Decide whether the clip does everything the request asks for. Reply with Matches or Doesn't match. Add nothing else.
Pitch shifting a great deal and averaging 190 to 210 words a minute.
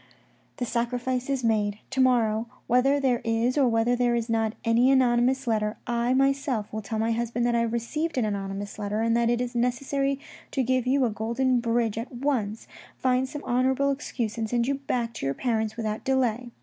Doesn't match